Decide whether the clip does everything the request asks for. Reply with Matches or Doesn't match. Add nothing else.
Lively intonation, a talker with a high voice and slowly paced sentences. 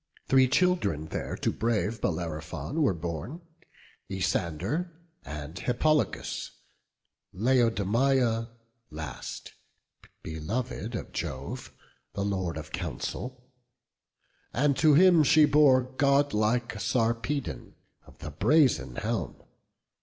Doesn't match